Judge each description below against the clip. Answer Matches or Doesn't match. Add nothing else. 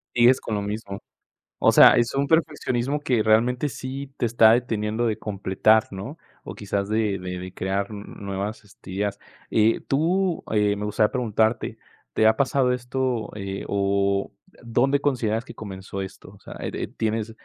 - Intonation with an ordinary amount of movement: Matches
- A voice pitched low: Matches